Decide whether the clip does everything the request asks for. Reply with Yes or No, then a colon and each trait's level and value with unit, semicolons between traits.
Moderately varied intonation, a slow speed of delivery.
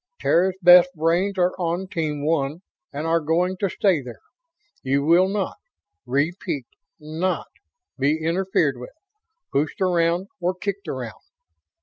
Yes: average, 3.7 semitones; slow, 130 wpm